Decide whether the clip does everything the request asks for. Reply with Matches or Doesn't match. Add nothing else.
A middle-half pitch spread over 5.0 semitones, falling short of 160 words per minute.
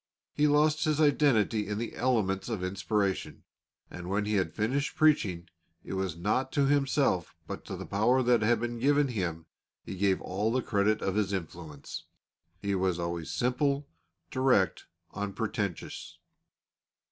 Matches